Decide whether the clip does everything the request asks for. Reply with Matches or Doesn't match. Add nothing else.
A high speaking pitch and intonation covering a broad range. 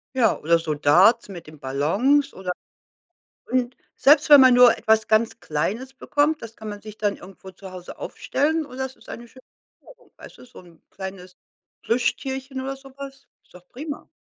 Matches